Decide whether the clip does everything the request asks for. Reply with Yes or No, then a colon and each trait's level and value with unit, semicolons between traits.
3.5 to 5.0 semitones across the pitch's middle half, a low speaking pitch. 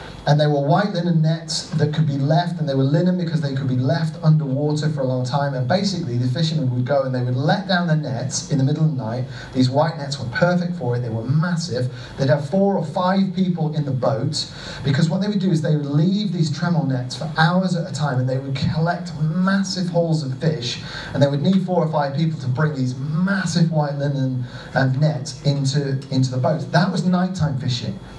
No: average, 3.9 semitones; medium, 150 Hz